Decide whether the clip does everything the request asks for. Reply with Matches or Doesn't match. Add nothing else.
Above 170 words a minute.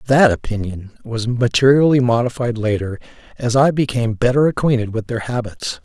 Doesn't match